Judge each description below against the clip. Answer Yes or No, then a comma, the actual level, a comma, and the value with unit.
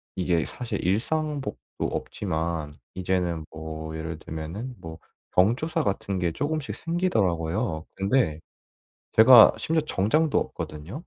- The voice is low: Yes, very low, 95 Hz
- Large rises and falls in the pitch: Yes, wide, 8.1 semitones